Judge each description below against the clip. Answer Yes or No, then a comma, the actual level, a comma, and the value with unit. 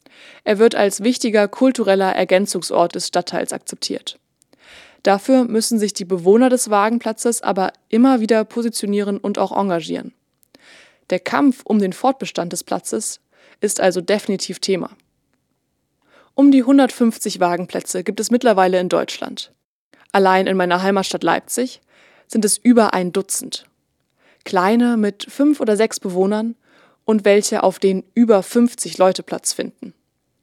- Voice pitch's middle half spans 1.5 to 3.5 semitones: No, average, 4.0 semitones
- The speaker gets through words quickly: No, average, 130 wpm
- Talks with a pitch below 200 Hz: No, high, 210 Hz